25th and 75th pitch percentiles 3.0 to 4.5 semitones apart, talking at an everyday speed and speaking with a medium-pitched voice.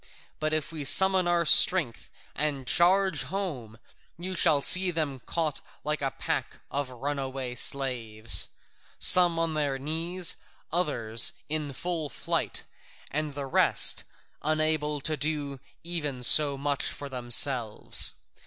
No: average, 3.6 semitones; slow, 125 wpm; medium, 150 Hz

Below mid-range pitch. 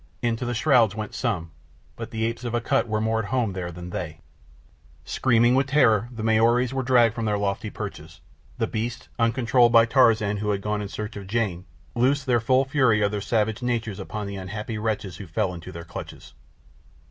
Yes: low, 110 Hz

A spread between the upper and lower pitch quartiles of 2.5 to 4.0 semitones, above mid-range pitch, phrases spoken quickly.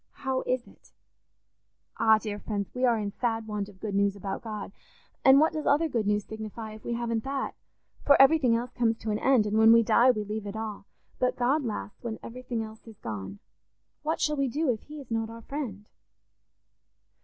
Yes: average, 3.3 semitones; high, 225 Hz; fast, 210 wpm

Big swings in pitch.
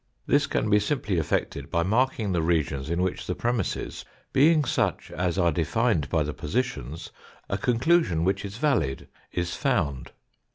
Yes: wide, 7.0 semitones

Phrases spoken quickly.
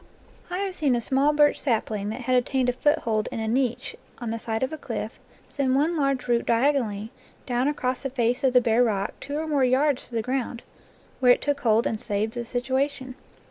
Yes: fast, 220 wpm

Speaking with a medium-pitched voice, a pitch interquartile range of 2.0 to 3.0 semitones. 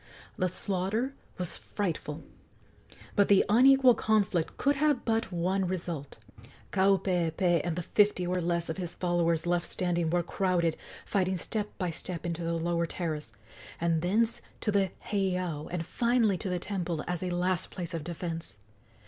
Yes: medium, 180 Hz; average, 2.7 semitones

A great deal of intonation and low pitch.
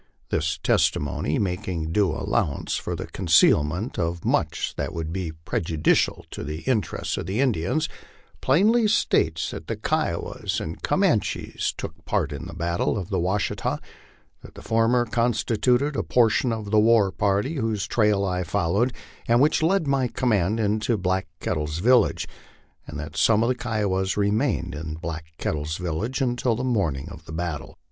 Yes: wide, 6.4 semitones; low, 100 Hz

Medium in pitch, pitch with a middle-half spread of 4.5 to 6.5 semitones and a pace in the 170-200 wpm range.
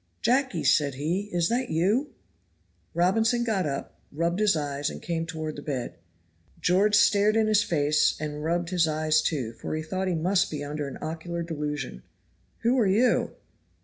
Yes: medium, 170 Hz; average, 5.2 semitones; average, 175 wpm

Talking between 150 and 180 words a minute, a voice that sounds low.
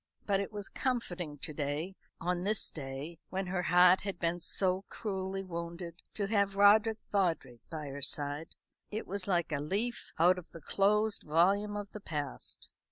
No: average, 170 wpm; medium, 180 Hz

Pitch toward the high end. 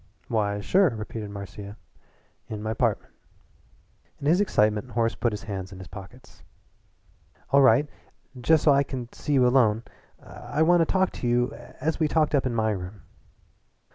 No: low, 120 Hz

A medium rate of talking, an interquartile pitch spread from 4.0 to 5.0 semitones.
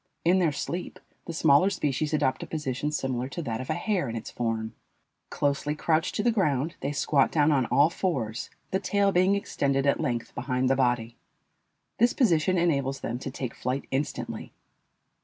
Yes: average, 180 wpm; average, 4.6 semitones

